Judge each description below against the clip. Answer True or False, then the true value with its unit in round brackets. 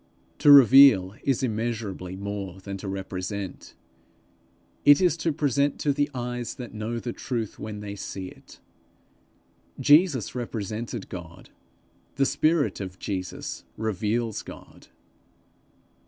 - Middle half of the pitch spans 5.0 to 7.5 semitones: True (5.6 semitones)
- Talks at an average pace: False (120 wpm)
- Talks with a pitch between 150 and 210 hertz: False (115 Hz)